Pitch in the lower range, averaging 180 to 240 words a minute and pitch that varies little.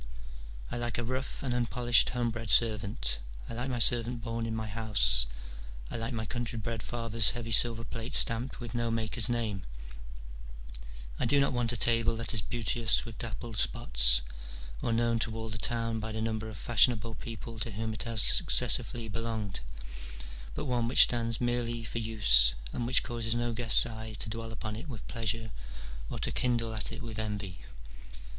Yes: low, 115 Hz; average, 185 wpm; narrow, 1.4 semitones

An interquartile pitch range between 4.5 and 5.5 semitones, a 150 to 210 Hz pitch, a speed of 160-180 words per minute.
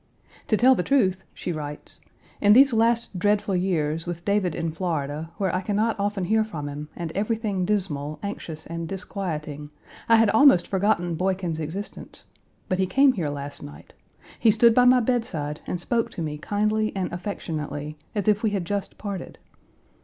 Yes: average, 4.9 semitones; high, 190 Hz; average, 175 wpm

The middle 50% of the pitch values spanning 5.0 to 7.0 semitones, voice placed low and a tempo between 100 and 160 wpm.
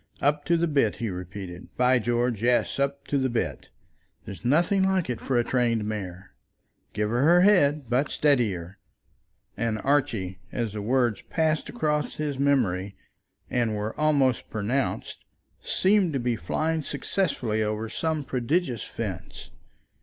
Yes: wide, 5.5 semitones; low, 125 Hz; average, 145 wpm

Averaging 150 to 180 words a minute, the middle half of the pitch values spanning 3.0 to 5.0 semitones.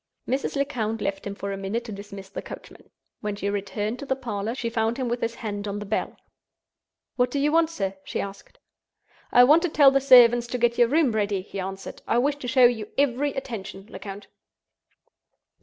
No: fast, 205 wpm; average, 4.3 semitones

